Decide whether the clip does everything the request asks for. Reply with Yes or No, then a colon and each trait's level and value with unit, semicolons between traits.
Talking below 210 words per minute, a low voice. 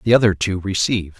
Yes: average, 200 wpm; low, 100 Hz